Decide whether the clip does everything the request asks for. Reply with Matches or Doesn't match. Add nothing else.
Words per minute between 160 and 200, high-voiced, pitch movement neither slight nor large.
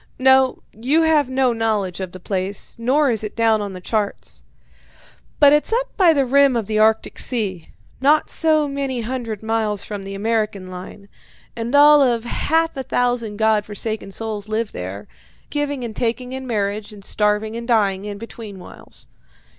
Matches